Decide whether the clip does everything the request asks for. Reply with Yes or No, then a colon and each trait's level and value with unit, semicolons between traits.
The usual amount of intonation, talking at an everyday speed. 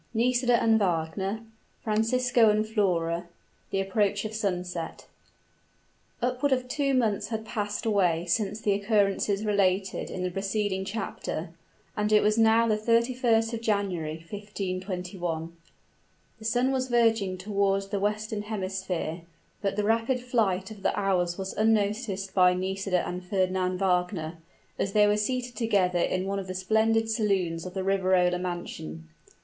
Yes: average, 3.2 semitones; average, 145 wpm